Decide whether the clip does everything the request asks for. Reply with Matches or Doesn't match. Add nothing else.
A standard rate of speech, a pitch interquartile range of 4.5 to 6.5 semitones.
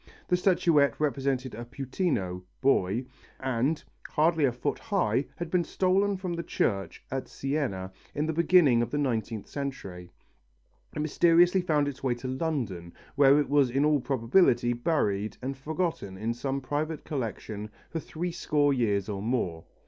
Matches